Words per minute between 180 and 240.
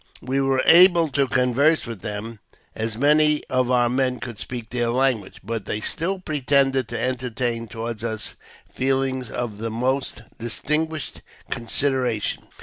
No: average, 150 wpm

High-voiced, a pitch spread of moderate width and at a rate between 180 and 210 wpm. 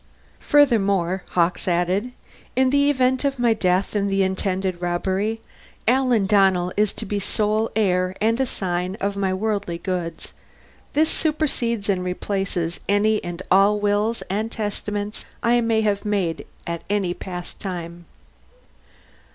No: high, 200 Hz; average, 3.3 semitones; slow, 135 wpm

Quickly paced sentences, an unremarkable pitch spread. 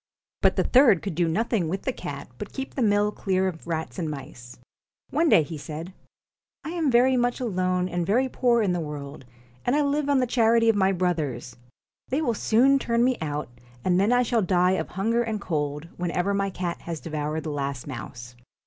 No: fast, 215 wpm; wide, 6.9 semitones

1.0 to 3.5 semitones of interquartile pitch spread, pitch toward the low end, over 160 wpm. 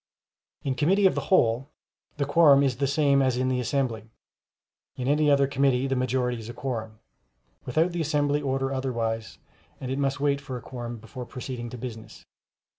Yes: narrow, 2.5 semitones; low, 130 Hz; average, 185 wpm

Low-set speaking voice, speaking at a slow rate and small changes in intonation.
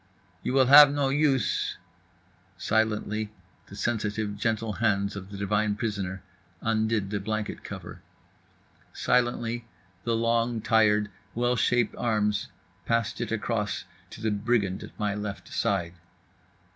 Yes: low, 110 Hz; slow, 125 wpm; narrow, 2.2 semitones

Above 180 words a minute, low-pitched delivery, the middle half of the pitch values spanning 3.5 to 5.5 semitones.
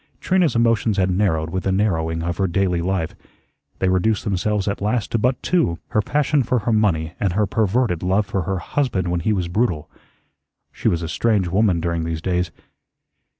Yes: average, 195 wpm; very low, 95 Hz; average, 3.9 semitones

